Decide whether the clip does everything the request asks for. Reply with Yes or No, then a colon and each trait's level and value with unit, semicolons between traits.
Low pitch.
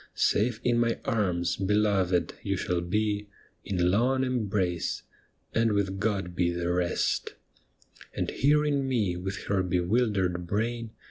Yes: low, 100 Hz